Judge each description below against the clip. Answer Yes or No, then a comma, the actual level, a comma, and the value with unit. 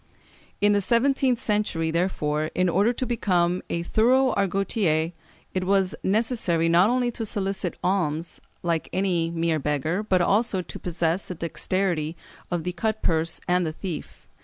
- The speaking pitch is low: No, medium, 185 Hz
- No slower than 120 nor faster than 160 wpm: Yes, average, 155 wpm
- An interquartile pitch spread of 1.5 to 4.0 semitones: Yes, average, 3.7 semitones